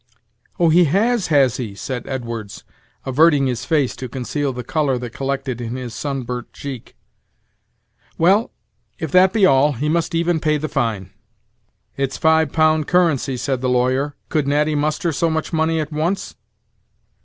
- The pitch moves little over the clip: No, average, 3.8 semitones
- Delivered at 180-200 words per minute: No, average, 160 wpm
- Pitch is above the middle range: No, medium, 145 Hz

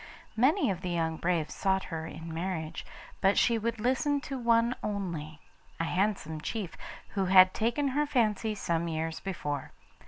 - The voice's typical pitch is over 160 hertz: Yes, high, 190 Hz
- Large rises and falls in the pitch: Yes, wide, 5.9 semitones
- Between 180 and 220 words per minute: No, average, 160 wpm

